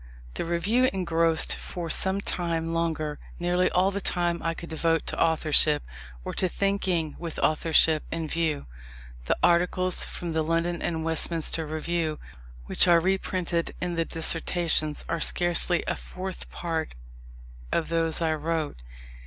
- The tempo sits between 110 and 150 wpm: Yes, average, 145 wpm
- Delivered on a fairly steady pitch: Yes, narrow, 1.5 semitones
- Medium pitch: Yes, medium, 165 Hz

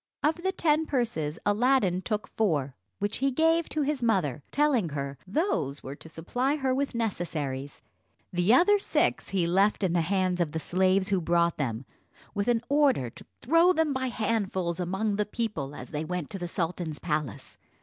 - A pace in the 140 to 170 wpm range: No, average, 180 wpm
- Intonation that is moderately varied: No, wide, 8.0 semitones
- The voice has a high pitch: Yes, high, 195 Hz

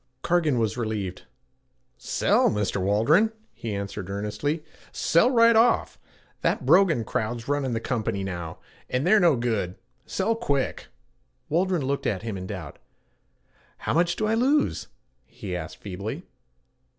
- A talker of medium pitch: No, low, 125 Hz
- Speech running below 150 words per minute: Yes, average, 140 wpm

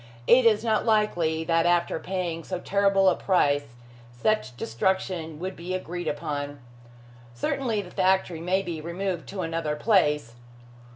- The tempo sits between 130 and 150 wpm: Yes, average, 140 wpm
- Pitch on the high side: No, medium, 175 Hz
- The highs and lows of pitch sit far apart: No, average, 3.3 semitones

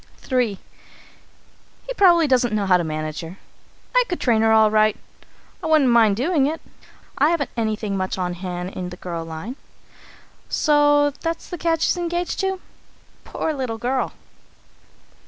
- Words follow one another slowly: No, average, 155 wpm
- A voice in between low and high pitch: No, high, 240 Hz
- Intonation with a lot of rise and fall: Yes, wide, 8.5 semitones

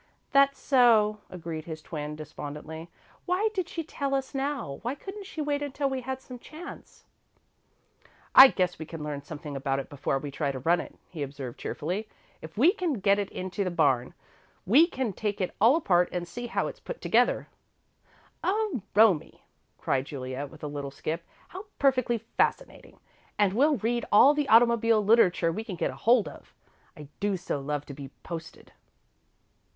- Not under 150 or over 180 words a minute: Yes, average, 175 wpm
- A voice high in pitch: Yes, high, 205 Hz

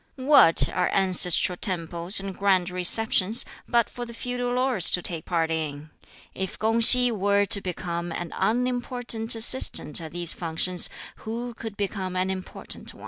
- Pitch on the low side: No, high, 190 Hz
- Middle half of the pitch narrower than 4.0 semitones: No, average, 4.7 semitones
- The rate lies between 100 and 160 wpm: Yes, average, 155 wpm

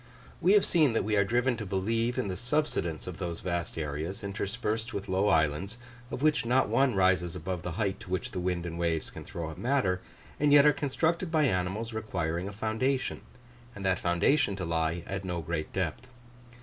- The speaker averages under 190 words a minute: No, average, 200 wpm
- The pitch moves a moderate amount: No, wide, 5.9 semitones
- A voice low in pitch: Yes, very low, 95 Hz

